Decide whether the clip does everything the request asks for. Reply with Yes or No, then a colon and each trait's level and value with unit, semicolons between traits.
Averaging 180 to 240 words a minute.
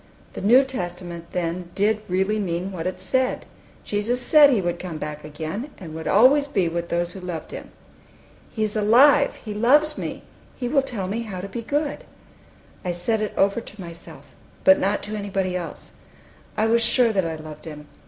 Yes: average, 195 wpm